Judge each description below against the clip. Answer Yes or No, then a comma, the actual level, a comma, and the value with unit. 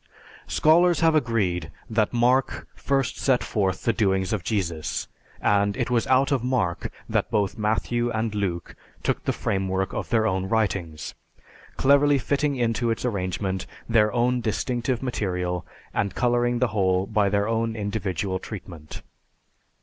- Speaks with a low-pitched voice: Yes, low, 110 Hz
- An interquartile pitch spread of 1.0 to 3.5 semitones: No, average, 4.2 semitones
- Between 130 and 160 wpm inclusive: Yes, average, 145 wpm